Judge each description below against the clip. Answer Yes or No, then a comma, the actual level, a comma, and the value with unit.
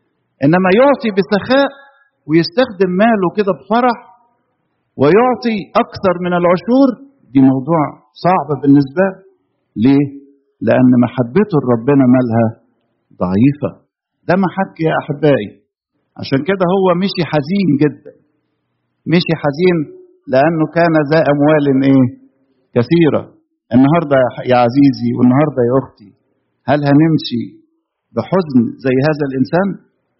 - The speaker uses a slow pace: Yes, slow, 105 wpm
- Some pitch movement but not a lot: No, wide, 6.3 semitones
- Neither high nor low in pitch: Yes, medium, 150 Hz